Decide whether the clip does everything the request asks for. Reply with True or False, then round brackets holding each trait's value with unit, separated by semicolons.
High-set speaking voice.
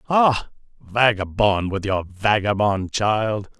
False (105 Hz)